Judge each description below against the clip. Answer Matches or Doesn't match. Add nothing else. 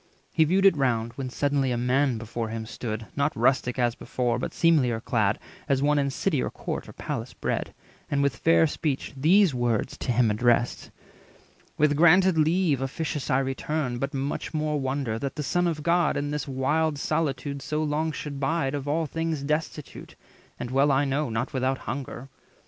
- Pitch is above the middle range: Doesn't match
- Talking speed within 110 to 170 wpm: Doesn't match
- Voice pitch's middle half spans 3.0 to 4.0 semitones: Matches